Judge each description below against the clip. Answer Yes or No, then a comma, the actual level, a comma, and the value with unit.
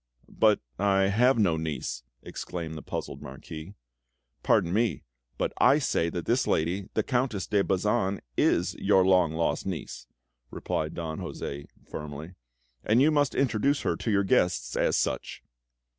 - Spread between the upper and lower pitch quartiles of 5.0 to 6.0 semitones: Yes, wide, 5.6 semitones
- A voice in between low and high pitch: No, very low, 95 Hz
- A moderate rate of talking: Yes, average, 150 wpm